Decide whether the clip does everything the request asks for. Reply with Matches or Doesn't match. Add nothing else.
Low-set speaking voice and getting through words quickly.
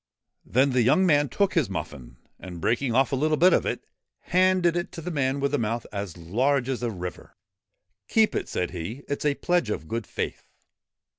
Matches